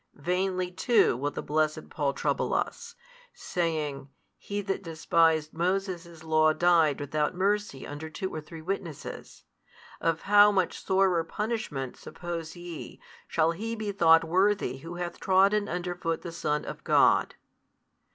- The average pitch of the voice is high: No, medium, 170 Hz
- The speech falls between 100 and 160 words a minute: Yes, average, 140 wpm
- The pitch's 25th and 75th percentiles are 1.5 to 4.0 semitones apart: Yes, average, 3.4 semitones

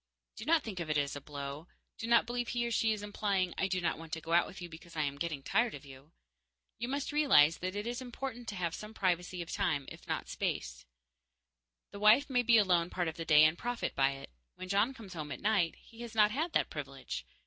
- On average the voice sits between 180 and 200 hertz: Yes, medium, 185 Hz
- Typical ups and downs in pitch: No, wide, 6.2 semitones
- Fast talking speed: Yes, fast, 255 wpm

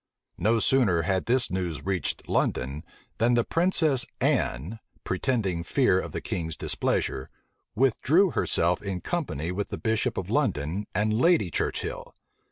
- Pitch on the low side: Yes, low, 100 Hz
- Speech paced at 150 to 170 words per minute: No, average, 140 wpm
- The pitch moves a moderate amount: No, wide, 6.6 semitones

